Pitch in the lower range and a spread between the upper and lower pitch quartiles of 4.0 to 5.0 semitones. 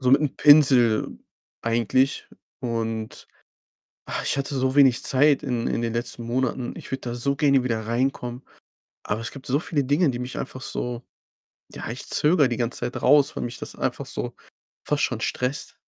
No: low, 130 Hz; average, 2.7 semitones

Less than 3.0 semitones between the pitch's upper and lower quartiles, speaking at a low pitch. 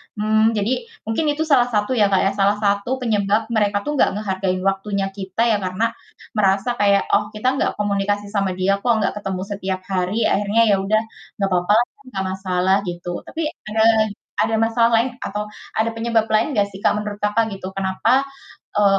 No: narrow, 2.4 semitones; high, 205 Hz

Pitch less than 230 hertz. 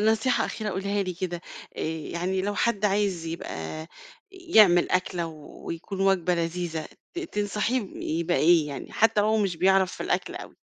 Yes: high, 190 Hz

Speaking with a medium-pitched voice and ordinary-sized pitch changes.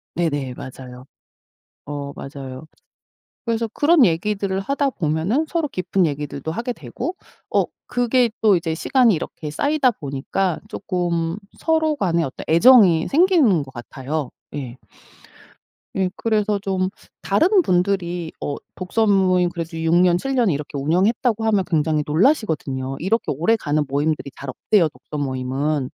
No: medium, 175 Hz; wide, 7.0 semitones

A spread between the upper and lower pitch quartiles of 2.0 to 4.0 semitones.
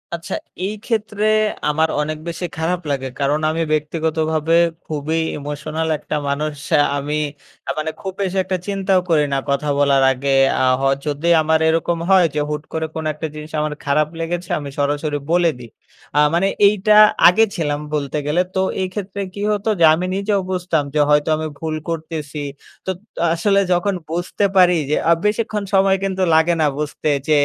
Yes: average, 3.6 semitones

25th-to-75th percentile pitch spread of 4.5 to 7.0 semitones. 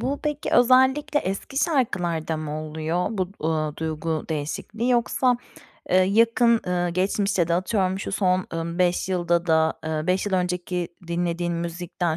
No: average, 3.9 semitones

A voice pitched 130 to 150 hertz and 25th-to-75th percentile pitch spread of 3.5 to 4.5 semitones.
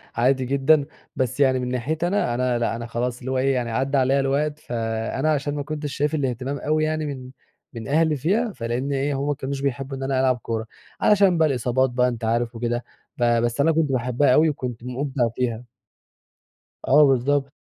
No: low, 135 Hz; average, 3.0 semitones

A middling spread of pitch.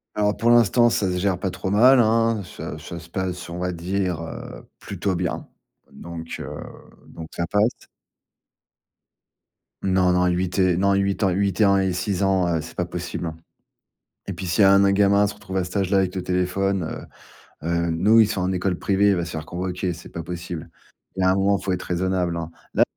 No: narrow, 2.0 semitones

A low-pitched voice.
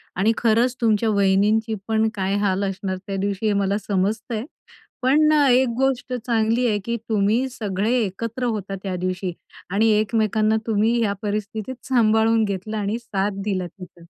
No: high, 215 Hz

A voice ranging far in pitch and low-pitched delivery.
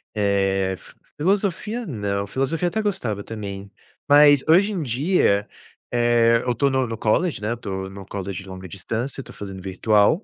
Yes: wide, 6.6 semitones; low, 115 Hz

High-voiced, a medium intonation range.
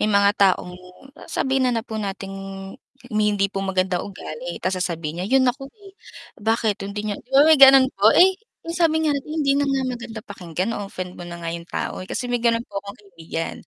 No: high, 205 Hz; wide, 5.8 semitones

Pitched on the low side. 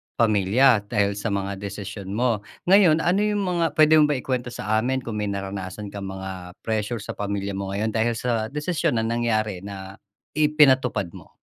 Yes: low, 110 Hz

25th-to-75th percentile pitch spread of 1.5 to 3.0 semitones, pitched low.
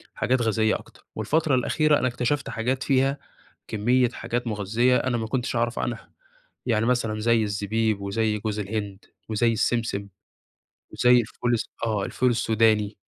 Yes: narrow, 2.5 semitones; low, 115 Hz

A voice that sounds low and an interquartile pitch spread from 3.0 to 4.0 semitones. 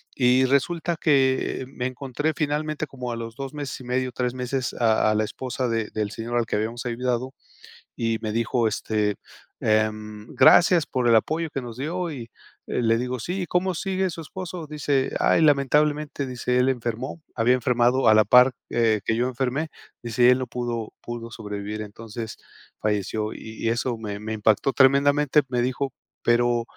Yes: low, 125 Hz; average, 3.4 semitones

